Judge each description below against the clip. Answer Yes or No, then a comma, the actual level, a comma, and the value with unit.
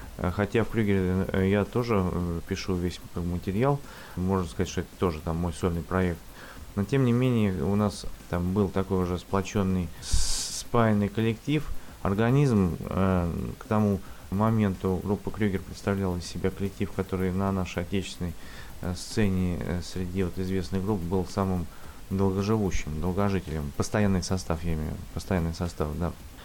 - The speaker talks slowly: No, average, 140 wpm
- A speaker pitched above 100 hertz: No, very low, 95 Hz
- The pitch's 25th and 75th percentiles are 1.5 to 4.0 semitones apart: Yes, narrow, 2.5 semitones